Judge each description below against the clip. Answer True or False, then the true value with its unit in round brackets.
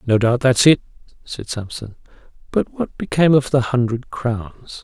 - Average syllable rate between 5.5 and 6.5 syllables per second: False (4.6 syllables/s)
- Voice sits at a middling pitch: False (125 Hz)